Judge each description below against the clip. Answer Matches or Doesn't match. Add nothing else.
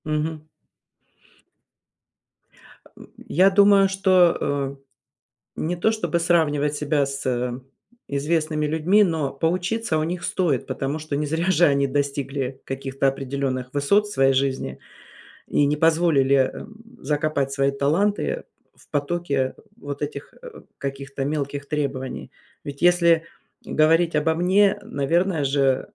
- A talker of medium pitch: Matches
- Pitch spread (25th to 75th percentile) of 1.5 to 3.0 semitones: Doesn't match